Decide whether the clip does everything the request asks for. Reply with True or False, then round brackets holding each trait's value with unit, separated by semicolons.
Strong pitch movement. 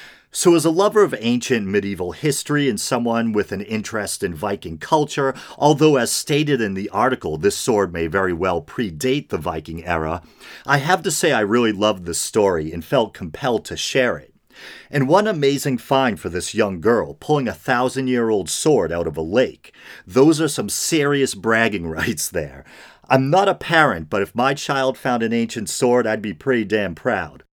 True (5.7 semitones)